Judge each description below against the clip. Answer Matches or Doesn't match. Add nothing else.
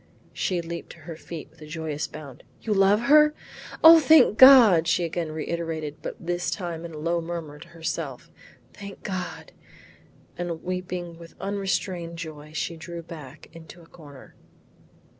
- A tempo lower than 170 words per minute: Matches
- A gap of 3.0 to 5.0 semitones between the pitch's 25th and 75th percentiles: Doesn't match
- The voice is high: Doesn't match